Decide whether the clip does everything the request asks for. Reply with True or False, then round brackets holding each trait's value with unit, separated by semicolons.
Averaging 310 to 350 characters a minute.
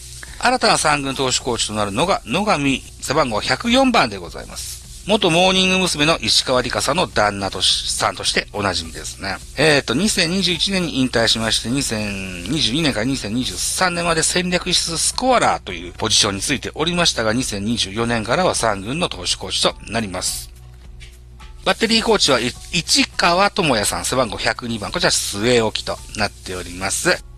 True (335 characters per minute)